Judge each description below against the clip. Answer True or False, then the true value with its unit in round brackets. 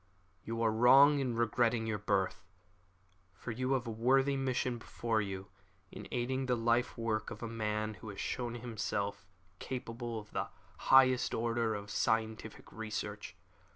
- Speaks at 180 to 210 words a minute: False (155 wpm)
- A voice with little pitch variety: True (2.3 semitones)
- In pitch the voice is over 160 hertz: False (115 Hz)